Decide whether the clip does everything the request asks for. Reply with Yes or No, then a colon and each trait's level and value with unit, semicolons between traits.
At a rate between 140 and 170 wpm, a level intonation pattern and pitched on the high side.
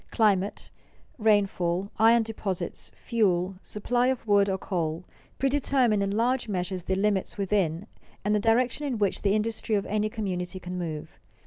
No: average, 150 wpm; average, 3.3 semitones; high, 205 Hz